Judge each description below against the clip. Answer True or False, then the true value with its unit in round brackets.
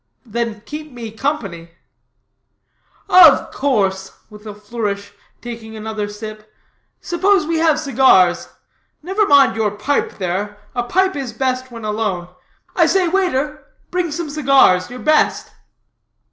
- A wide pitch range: True (6.4 semitones)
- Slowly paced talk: True (130 wpm)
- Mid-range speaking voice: False (240 Hz)